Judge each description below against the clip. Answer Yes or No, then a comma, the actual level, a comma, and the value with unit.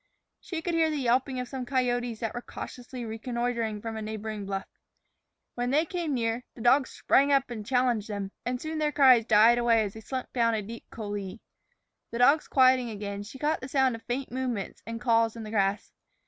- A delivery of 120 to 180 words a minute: No, fast, 205 wpm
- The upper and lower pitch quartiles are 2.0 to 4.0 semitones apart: Yes, average, 2.9 semitones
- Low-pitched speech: No, high, 240 Hz